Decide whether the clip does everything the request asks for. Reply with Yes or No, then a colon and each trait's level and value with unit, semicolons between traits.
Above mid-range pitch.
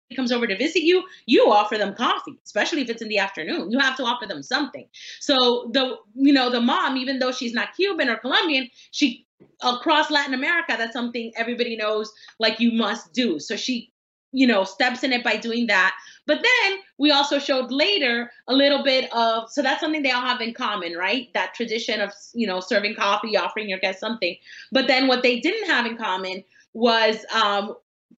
Yes: high, 245 Hz